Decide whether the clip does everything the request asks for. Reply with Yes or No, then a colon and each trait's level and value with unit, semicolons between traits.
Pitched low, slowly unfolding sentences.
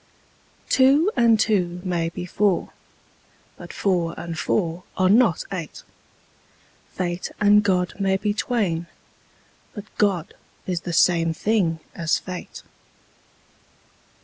No: medium, 185 Hz; slow, 115 wpm